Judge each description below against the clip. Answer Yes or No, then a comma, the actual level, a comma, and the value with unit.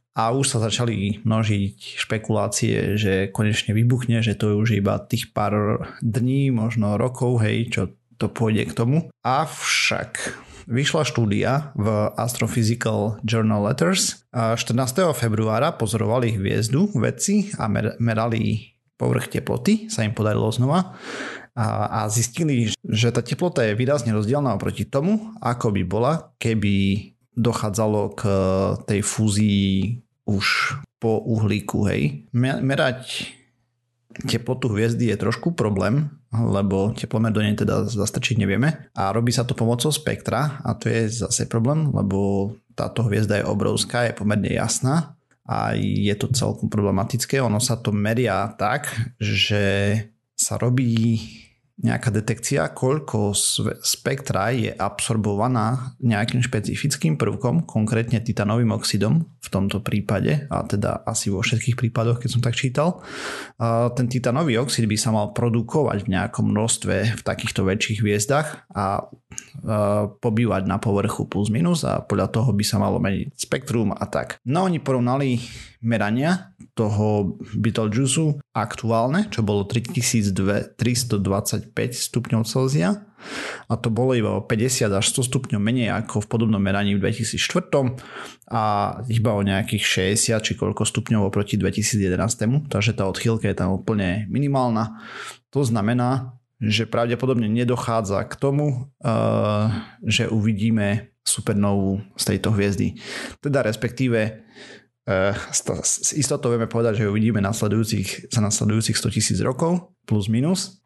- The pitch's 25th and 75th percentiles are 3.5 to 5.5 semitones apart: No, average, 3.0 semitones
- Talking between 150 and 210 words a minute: No, average, 130 wpm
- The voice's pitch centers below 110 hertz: No, low, 115 Hz